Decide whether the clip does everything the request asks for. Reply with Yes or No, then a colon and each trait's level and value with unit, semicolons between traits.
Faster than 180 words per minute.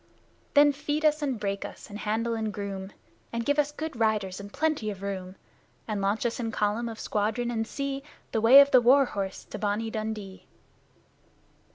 Yes: average, 190 wpm